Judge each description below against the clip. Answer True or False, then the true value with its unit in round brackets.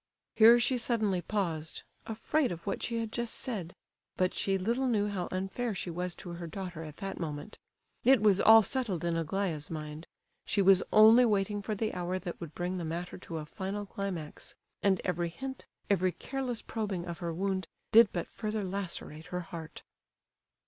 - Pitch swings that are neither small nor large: True (4.0 semitones)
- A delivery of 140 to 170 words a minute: False (185 wpm)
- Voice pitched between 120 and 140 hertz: False (190 Hz)